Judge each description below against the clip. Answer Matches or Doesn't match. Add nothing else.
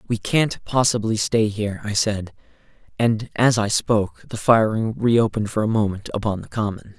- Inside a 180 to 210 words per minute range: Doesn't match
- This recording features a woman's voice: Doesn't match